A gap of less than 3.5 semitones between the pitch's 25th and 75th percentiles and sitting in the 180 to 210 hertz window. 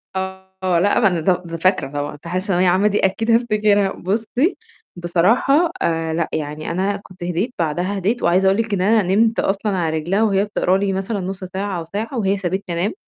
Yes: average, 2.8 semitones; high, 190 Hz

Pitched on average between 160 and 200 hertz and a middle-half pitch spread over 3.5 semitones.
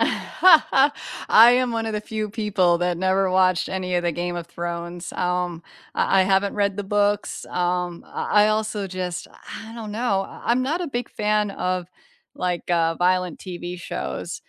No: high, 190 Hz; average, 3.1 semitones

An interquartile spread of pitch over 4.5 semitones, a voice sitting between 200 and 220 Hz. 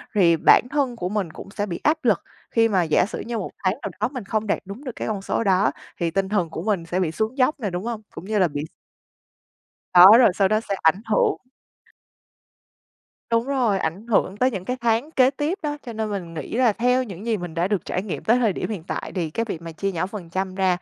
No: average, 4.2 semitones; high, 205 Hz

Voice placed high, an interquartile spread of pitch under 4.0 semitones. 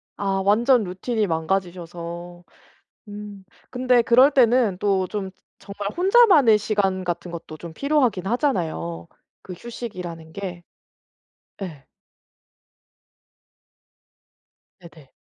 No: high, 195 Hz; average, 5.2 semitones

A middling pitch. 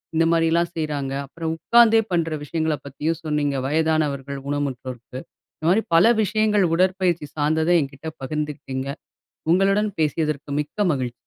Yes: medium, 155 Hz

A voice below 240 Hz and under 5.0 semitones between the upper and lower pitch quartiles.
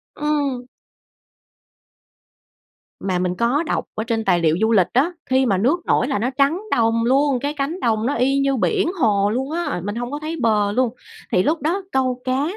No: very high, 255 Hz; average, 4.6 semitones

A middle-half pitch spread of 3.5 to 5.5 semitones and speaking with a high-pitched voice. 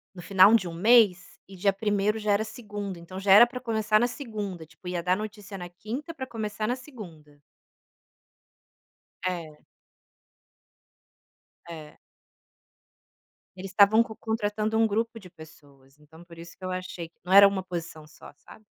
Yes: average, 3.8 semitones; high, 200 Hz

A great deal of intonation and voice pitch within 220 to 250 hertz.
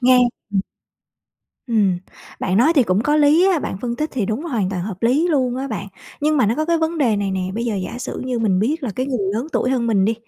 Yes: wide, 5.9 semitones; high, 240 Hz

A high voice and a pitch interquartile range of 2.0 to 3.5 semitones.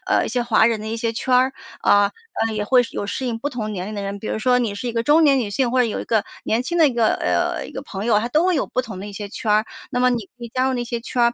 Yes: high, 235 Hz; average, 2.9 semitones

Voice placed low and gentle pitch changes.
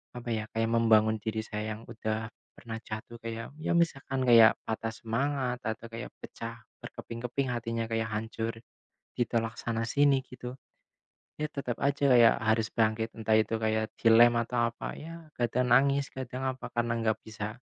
Yes: low, 115 Hz; narrow, 1.9 semitones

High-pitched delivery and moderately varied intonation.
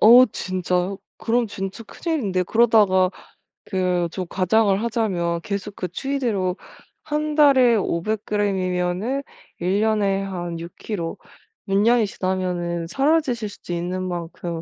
Yes: high, 195 Hz; average, 3.9 semitones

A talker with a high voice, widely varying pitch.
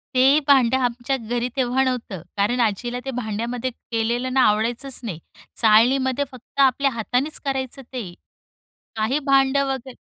No: very high, 250 Hz; narrow, 2.5 semitones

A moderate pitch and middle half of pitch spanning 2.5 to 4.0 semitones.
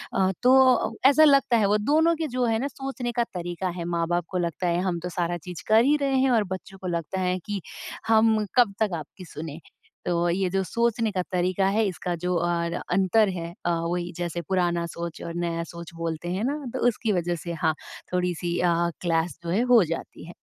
No: medium, 180 Hz; average, 4.7 semitones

